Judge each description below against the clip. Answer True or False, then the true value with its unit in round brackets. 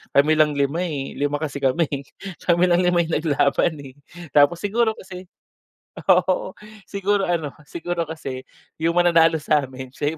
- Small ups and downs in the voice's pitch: False (3.6 semitones)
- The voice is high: False (160 Hz)